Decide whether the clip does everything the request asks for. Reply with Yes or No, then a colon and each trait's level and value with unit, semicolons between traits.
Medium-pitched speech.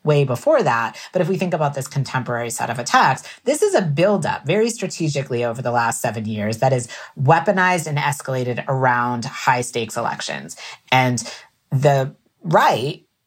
No: low, 130 Hz